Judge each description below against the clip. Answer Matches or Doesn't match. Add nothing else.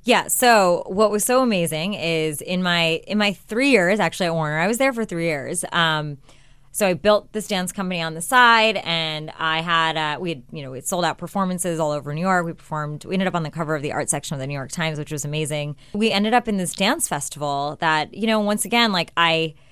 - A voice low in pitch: Doesn't match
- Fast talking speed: Matches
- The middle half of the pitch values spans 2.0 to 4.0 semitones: Doesn't match